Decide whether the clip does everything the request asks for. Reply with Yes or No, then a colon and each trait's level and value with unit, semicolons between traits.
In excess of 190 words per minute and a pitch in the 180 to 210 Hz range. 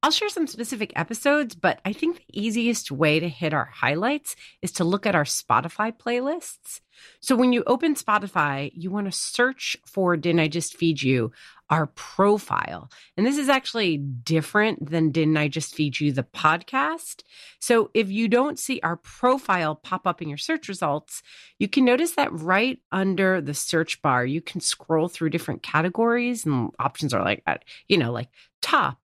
No: average, 180 wpm; medium, 185 Hz